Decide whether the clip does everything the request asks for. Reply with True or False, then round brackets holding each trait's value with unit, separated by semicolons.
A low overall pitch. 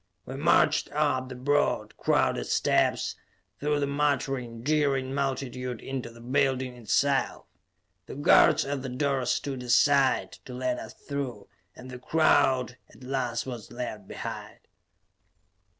True (130 Hz)